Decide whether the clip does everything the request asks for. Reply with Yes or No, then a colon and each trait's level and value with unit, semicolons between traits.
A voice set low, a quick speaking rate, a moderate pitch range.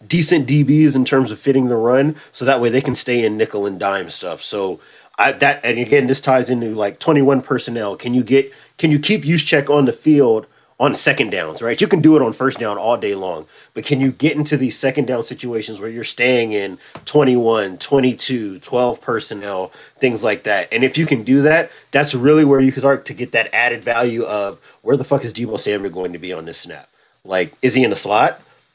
Yes: low, 130 Hz; fast, 230 wpm; average, 3.5 semitones